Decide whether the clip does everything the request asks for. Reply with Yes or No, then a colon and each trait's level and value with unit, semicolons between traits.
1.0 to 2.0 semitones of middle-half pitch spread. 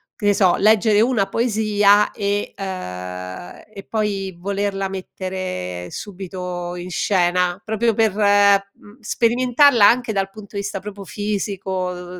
No: narrow, 2.4 semitones